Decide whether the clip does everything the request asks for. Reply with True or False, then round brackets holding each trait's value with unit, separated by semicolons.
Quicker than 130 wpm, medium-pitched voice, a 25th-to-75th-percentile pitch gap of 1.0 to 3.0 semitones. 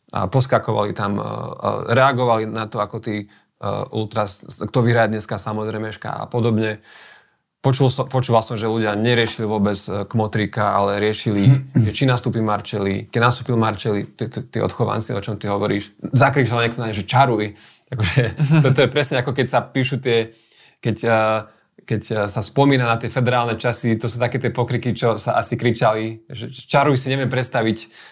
False (160 wpm; 115 Hz; 2.7 semitones)